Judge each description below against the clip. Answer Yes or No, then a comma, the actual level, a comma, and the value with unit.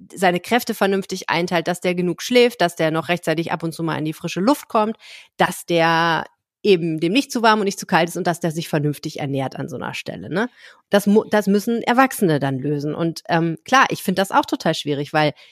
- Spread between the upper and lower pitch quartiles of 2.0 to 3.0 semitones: No, average, 4.2 semitones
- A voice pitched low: No, medium, 175 Hz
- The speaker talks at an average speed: No, fast, 230 wpm